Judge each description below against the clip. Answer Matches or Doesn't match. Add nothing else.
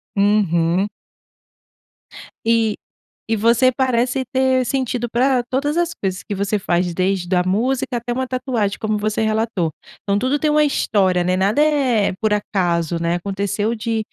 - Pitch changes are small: Doesn't match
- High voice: Matches